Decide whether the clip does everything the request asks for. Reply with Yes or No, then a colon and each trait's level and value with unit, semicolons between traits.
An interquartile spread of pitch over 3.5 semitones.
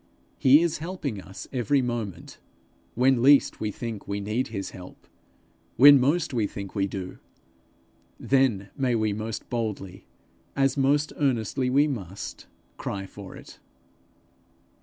Yes: average, 5.3 semitones